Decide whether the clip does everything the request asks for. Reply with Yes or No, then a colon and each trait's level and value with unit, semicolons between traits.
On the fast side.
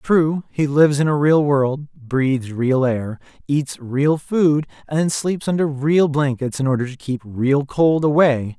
No: average, 175 wpm